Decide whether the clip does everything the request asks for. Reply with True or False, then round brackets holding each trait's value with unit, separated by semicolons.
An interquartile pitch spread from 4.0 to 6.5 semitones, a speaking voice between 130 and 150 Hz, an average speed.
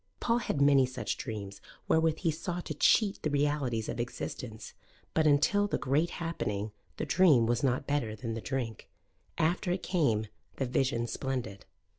True (5.5 semitones; 140 Hz; 165 wpm)